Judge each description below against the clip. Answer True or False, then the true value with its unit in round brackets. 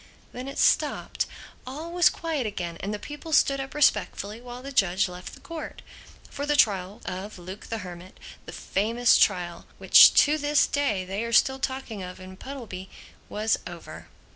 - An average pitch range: False (6.6 semitones)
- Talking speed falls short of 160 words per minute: False (175 wpm)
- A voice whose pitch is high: True (225 Hz)